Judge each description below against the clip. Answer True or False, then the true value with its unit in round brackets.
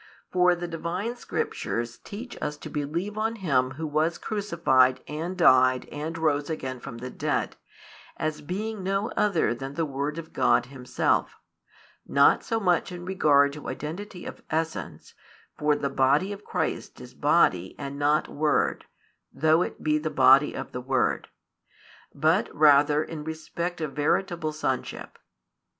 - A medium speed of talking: True (150 wpm)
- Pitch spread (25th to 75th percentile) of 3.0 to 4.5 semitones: True (3.9 semitones)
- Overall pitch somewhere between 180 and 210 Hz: False (155 Hz)